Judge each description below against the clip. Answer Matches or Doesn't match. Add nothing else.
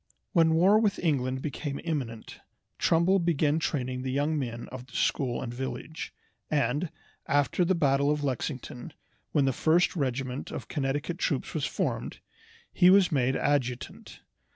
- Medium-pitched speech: Matches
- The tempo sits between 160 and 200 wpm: Doesn't match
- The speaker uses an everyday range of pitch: Matches